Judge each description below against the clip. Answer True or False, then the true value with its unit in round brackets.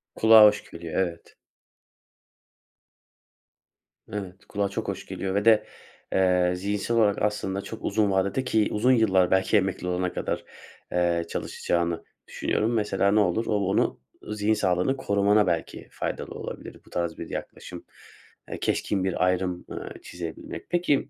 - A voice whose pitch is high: False (100 Hz)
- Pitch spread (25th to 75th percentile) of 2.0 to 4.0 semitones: True (2.8 semitones)